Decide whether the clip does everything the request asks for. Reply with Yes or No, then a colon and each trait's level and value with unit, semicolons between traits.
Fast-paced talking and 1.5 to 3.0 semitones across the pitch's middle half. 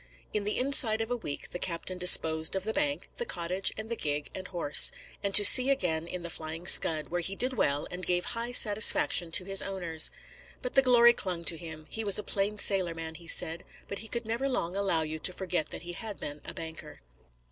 No: fast, 230 wpm; average, 5.0 semitones